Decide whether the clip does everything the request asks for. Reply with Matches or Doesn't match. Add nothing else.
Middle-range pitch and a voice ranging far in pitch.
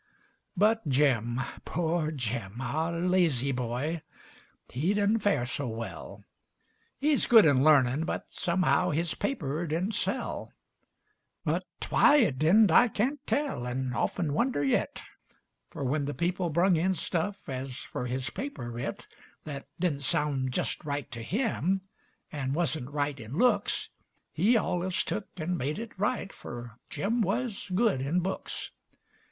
Matches